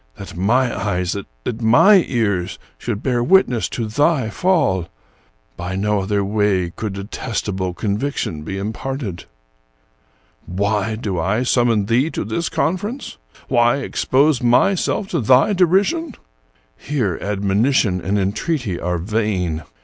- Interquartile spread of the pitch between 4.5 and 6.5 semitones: Yes, wide, 5.5 semitones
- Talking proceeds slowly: Yes, slow, 130 wpm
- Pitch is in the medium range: No, low, 110 Hz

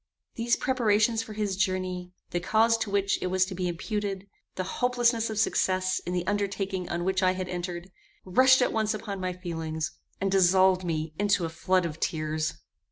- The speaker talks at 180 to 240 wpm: Yes, average, 185 wpm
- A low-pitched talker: No, medium, 185 Hz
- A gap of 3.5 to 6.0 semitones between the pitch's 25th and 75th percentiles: No, average, 2.8 semitones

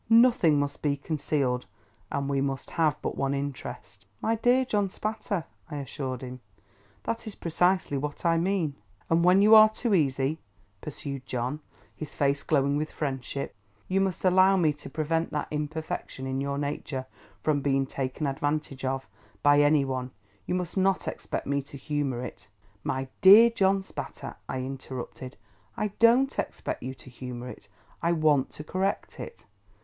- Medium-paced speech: Yes, average, 165 wpm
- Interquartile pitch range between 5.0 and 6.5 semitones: Yes, wide, 5.4 semitones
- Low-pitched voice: No, medium, 145 Hz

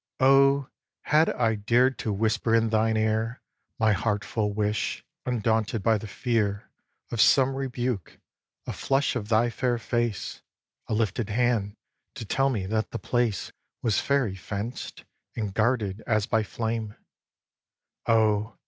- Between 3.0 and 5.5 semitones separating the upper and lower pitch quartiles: No, narrow, 2.4 semitones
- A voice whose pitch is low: Yes, low, 110 Hz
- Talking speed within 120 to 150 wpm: Yes, average, 145 wpm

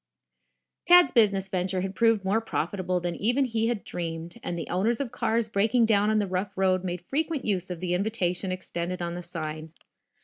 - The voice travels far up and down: No, average, 4.1 semitones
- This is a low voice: No, high, 195 Hz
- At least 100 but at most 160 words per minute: No, average, 195 wpm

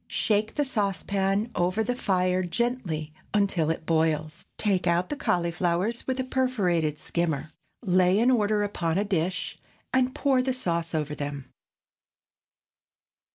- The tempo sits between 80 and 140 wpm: Yes, slow, 135 wpm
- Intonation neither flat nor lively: Yes, average, 4.9 semitones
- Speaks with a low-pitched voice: No, medium, 185 Hz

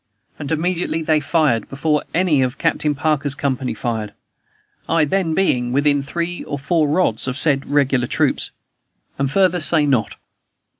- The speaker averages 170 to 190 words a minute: No, average, 150 wpm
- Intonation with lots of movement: No, average, 3.2 semitones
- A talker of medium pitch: Yes, medium, 145 Hz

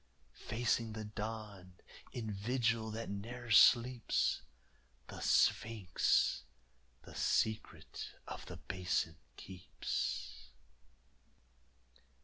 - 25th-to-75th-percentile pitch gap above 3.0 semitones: Yes, average, 3.5 semitones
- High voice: No, low, 110 Hz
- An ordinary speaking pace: No, slow, 80 wpm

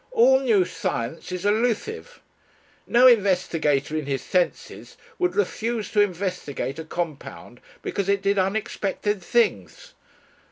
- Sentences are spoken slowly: Yes, slow, 120 wpm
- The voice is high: Yes, high, 195 Hz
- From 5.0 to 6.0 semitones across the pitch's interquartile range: Yes, wide, 5.5 semitones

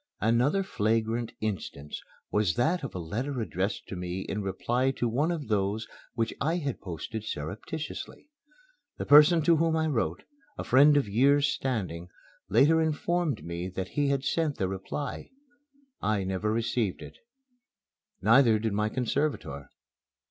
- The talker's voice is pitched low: Yes, low, 115 Hz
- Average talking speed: Yes, average, 150 wpm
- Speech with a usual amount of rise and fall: No, wide, 6.6 semitones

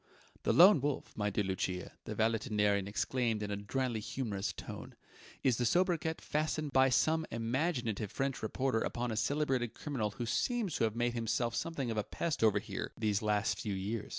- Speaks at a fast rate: No, average, 180 wpm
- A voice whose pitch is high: No, low, 115 Hz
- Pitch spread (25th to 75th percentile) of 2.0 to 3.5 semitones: No, average, 4.4 semitones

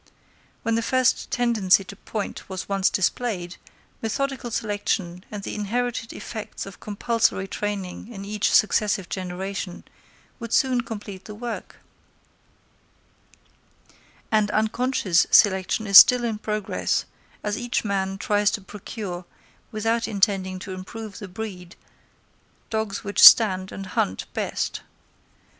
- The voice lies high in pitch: Yes, high, 205 Hz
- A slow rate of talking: Yes, slow, 120 wpm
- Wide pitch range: No, average, 2.9 semitones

